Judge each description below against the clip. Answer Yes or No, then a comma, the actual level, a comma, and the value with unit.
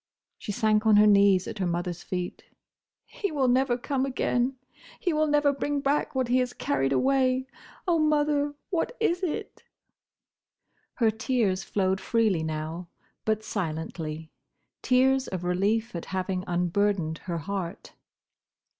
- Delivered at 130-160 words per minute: Yes, slow, 135 wpm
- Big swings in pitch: Yes, wide, 6.9 semitones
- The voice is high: Yes, high, 220 Hz